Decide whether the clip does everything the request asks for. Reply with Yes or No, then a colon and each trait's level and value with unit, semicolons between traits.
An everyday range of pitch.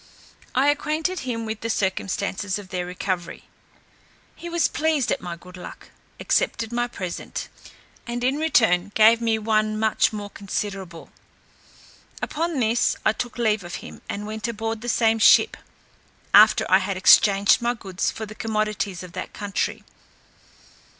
Yes: average, 3.3 semitones